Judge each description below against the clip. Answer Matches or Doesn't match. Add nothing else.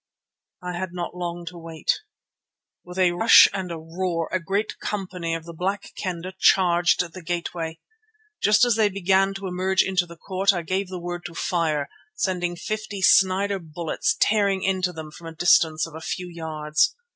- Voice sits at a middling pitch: Matches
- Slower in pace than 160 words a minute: Doesn't match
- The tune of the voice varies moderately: Doesn't match